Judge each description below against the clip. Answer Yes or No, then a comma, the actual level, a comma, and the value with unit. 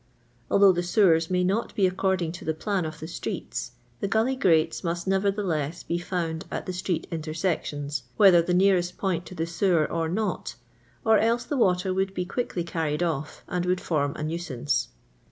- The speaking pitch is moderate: Yes, medium, 175 Hz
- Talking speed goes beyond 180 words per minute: Yes, average, 190 wpm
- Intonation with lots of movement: No, average, 2.9 semitones